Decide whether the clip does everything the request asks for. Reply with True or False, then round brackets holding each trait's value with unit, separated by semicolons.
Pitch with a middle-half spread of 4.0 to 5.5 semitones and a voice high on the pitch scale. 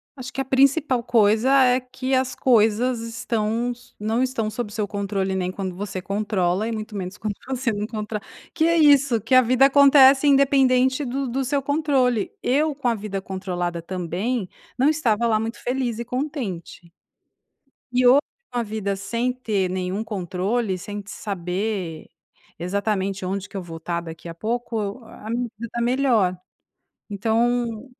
True (4.5 semitones; 225 Hz)